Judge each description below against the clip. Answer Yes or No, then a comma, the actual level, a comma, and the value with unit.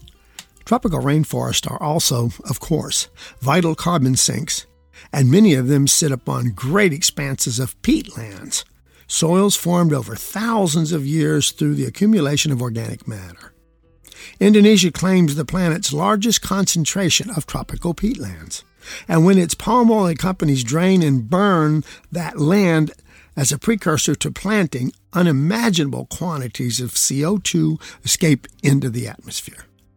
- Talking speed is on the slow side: Yes, slow, 130 wpm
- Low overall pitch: No, medium, 155 Hz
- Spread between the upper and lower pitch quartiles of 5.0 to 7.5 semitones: Yes, wide, 5.6 semitones